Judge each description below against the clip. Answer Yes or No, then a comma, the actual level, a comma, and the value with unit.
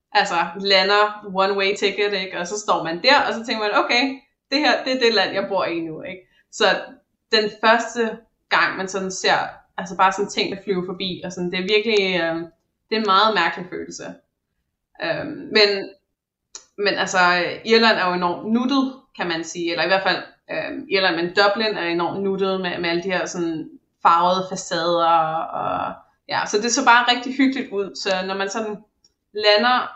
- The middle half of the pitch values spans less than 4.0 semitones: Yes, average, 3.6 semitones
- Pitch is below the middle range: No, high, 195 Hz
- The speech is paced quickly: No, average, 195 wpm